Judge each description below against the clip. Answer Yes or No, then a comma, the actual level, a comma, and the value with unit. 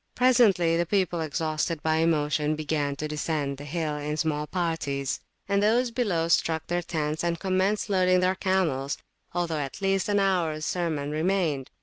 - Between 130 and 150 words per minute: No, average, 160 wpm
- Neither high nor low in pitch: Yes, medium, 165 Hz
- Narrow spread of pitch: No, average, 3.7 semitones